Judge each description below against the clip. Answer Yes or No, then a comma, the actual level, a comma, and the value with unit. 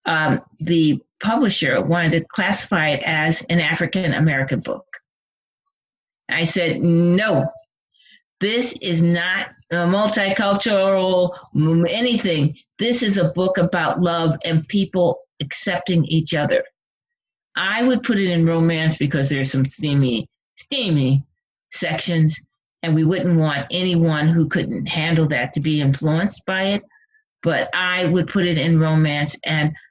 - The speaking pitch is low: No, medium, 170 Hz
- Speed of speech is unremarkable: No, slow, 130 wpm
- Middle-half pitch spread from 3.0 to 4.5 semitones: Yes, average, 3.5 semitones